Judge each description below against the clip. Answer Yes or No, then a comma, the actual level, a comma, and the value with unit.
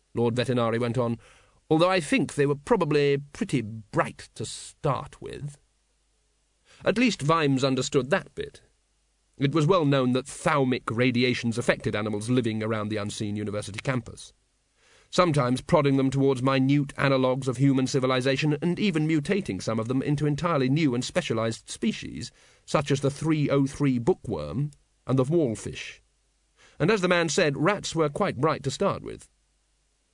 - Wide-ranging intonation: No, average, 3.5 semitones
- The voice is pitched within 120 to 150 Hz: Yes, low, 135 Hz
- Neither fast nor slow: Yes, average, 155 wpm